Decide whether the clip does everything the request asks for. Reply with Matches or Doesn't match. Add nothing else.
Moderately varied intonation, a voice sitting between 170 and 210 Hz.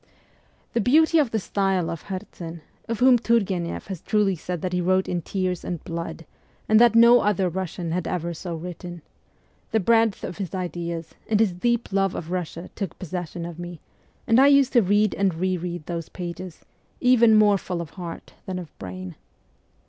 Matches